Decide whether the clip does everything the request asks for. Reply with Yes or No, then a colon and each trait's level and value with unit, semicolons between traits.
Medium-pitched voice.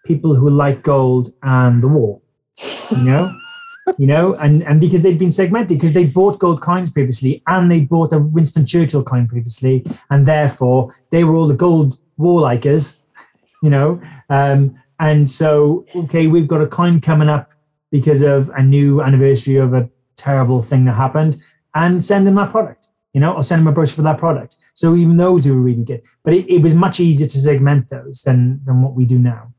Yes: medium, 150 Hz